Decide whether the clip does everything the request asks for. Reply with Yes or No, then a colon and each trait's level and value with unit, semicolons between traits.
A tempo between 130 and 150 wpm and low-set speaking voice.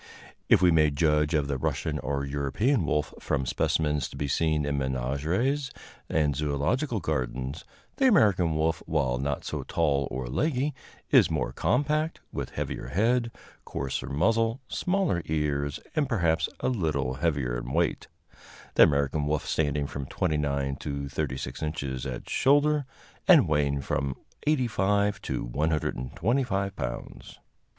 Yes: average, 140 wpm; very low, 75 Hz